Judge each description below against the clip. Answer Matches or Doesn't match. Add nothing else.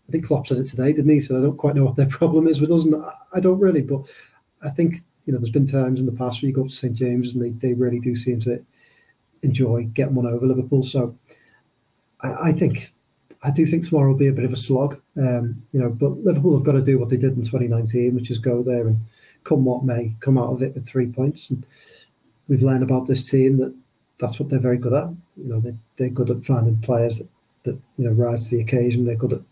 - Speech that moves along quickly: Matches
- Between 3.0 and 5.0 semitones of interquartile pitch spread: Doesn't match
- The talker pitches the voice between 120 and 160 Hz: Matches